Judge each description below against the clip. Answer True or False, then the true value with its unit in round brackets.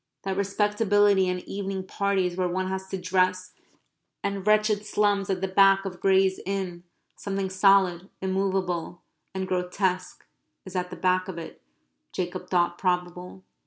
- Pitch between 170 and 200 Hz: True (190 Hz)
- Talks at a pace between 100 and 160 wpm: True (145 wpm)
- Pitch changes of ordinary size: False (1.3 semitones)